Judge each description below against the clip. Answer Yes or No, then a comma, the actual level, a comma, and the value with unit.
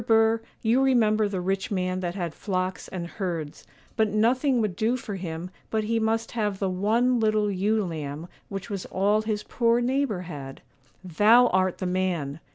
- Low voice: No, high, 205 Hz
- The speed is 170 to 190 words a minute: Yes, average, 175 wpm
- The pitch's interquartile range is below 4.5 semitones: Yes, average, 3.4 semitones